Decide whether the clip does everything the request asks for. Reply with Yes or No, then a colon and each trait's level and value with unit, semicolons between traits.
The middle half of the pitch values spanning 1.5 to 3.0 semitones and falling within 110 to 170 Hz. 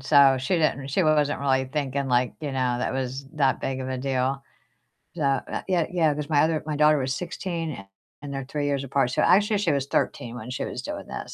Yes: narrow, 2.6 semitones; medium, 140 Hz